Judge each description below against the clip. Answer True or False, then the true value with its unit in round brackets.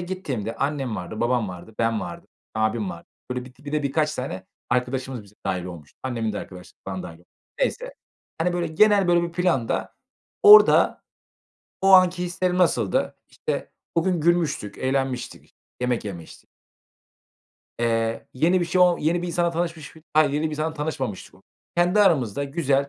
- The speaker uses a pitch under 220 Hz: True (140 Hz)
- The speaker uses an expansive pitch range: True (7.3 semitones)